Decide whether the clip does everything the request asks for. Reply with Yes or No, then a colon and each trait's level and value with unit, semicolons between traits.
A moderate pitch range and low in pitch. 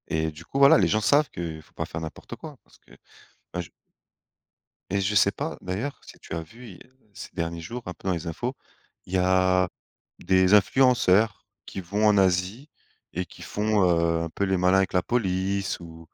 Yes: average, 3.5 semitones; very low, 95 Hz